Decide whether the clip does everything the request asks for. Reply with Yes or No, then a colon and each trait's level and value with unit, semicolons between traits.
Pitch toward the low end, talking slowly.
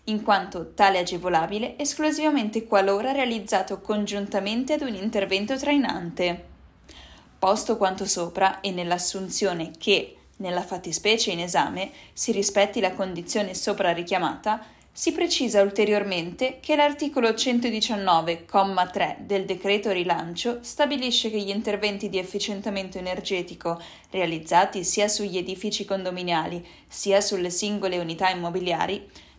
No: high, 200 Hz; slow, 110 wpm